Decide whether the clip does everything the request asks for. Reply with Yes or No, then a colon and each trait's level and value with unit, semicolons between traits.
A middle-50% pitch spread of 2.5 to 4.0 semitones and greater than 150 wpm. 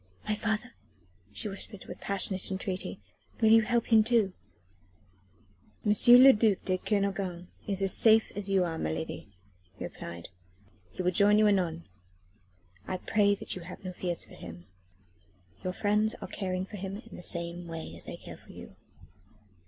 Yes: average, 2.8 semitones; average, 170 wpm